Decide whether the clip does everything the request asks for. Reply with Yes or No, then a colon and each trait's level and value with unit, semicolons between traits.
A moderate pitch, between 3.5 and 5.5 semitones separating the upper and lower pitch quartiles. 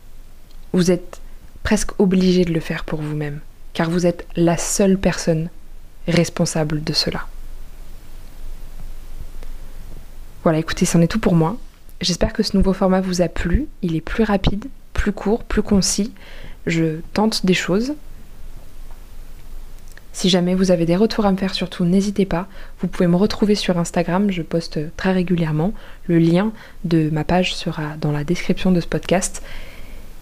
No: medium, 180 Hz; average, 2.7 semitones